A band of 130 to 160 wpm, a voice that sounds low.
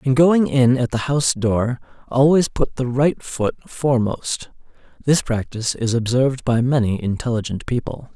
Yes: average, 155 wpm; low, 125 Hz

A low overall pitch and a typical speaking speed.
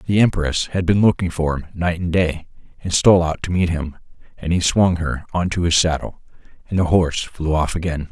No: very low, 85 Hz; fast, 220 wpm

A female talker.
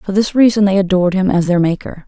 Yes: female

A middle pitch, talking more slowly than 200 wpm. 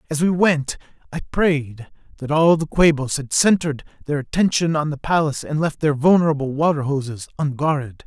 Yes: medium, 150 Hz; average, 170 wpm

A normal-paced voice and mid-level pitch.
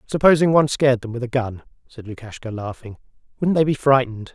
No: average, 195 wpm; low, 125 Hz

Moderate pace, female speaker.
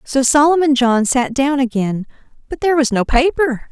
Yes: average, 180 wpm; female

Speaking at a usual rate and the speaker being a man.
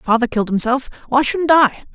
No: average, 155 wpm; female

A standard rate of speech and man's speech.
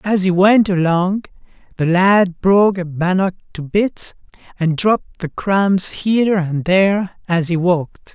Yes: average, 155 wpm; male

